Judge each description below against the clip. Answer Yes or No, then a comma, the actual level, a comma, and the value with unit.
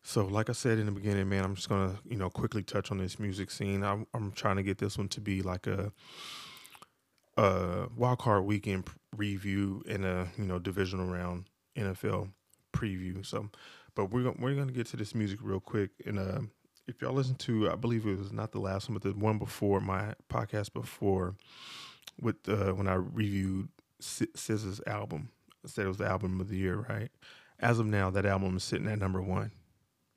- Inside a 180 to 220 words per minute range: Yes, average, 200 wpm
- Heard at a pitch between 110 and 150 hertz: No, low, 100 Hz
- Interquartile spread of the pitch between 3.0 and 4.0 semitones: No, narrow, 2.4 semitones